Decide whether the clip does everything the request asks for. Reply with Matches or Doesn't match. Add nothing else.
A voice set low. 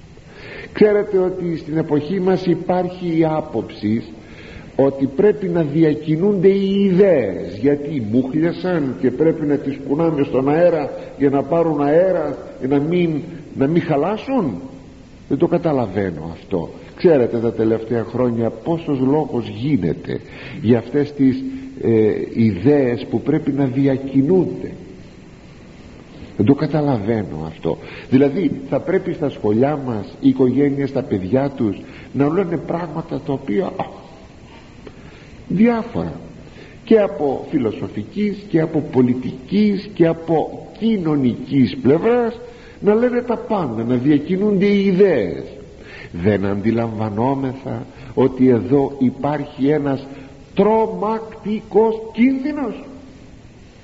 Doesn't match